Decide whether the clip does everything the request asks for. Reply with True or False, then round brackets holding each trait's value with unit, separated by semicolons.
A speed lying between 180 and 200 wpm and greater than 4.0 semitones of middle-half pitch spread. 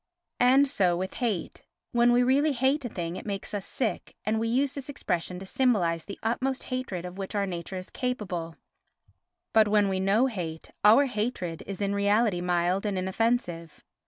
True (190 wpm; 5.2 semitones)